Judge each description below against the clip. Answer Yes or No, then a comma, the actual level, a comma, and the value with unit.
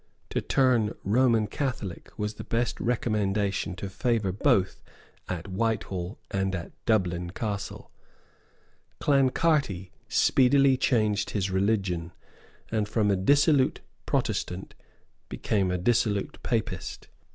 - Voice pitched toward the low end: Yes, low, 105 Hz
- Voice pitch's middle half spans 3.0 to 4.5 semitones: Yes, average, 3.9 semitones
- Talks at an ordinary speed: No, slow, 105 wpm